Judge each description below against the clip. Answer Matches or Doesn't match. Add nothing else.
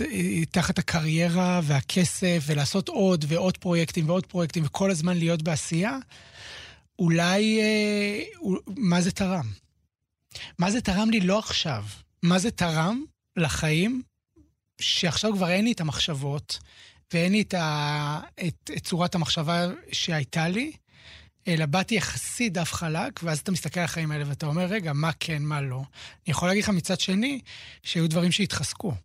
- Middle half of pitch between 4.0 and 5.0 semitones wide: Doesn't match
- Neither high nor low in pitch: Matches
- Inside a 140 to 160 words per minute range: Matches